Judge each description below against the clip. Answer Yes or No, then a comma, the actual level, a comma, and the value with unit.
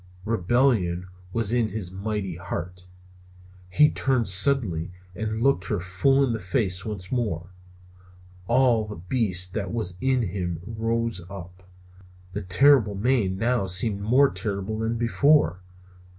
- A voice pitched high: No, low, 105 Hz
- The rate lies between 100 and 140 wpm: Yes, slow, 135 wpm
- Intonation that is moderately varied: Yes, average, 4.4 semitones